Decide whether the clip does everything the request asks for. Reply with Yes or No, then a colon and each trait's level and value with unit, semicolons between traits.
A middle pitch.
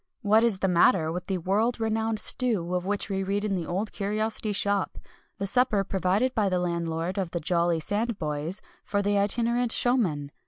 No: high, 200 Hz